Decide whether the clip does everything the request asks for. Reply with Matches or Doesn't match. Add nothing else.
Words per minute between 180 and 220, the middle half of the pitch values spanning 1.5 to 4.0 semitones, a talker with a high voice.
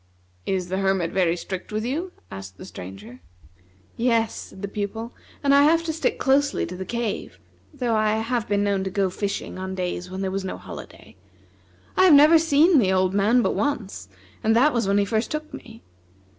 Doesn't match